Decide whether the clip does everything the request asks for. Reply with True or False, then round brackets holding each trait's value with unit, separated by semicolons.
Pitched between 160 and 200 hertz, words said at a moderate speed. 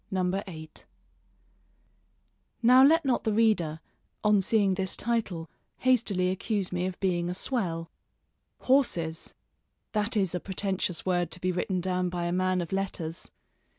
True (185 Hz; 150 wpm)